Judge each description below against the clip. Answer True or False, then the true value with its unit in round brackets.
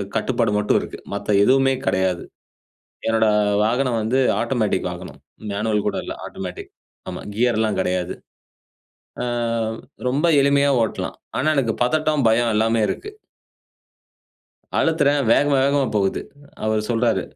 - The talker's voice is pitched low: True (115 Hz)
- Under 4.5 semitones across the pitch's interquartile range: True (4.0 semitones)